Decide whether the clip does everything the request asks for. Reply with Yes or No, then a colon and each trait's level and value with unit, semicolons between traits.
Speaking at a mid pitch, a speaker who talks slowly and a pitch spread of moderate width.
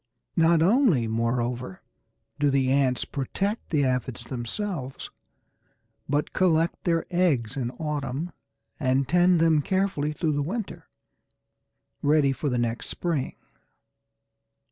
Yes: medium, 145 Hz; slow, 115 wpm; average, 4.8 semitones